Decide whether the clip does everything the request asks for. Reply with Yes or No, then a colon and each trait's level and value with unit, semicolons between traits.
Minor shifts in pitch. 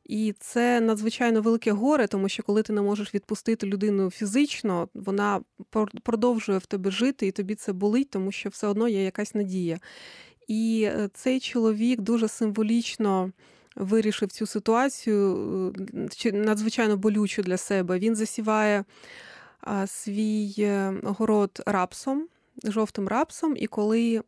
Yes: narrow, 2.1 semitones